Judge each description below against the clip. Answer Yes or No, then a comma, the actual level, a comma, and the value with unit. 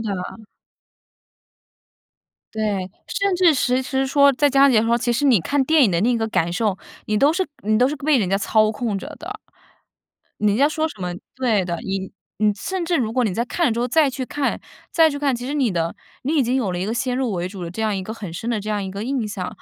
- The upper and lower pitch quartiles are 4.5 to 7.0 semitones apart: Yes, average, 5.2 semitones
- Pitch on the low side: No, high, 235 Hz